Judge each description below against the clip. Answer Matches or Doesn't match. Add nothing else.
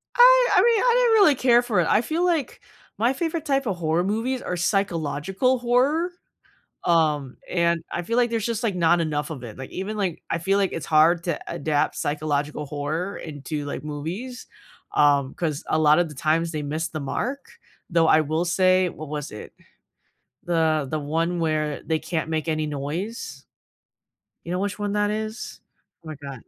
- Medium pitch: Matches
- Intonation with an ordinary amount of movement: Doesn't match